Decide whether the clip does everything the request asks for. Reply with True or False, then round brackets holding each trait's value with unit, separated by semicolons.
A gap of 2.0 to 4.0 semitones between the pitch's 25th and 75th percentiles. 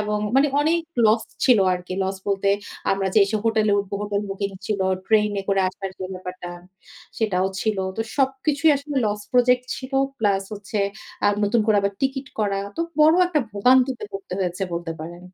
False (4.4 semitones)